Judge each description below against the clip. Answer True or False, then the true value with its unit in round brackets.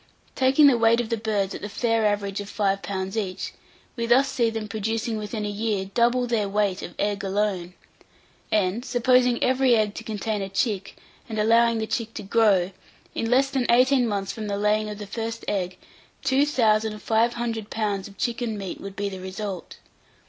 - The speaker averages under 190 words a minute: False (195 wpm)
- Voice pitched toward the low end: False (215 Hz)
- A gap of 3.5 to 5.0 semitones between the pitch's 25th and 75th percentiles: False (2.7 semitones)